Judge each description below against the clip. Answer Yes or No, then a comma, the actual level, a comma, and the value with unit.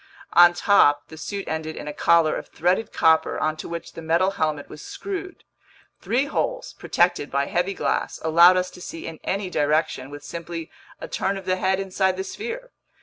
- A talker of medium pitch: Yes, medium, 175 Hz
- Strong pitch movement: No, average, 3.5 semitones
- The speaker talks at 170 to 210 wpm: Yes, average, 190 wpm